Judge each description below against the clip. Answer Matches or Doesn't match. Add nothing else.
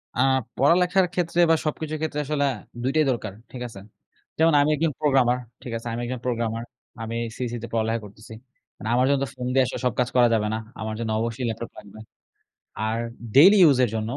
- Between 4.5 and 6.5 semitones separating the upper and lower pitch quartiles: Matches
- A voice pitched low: Matches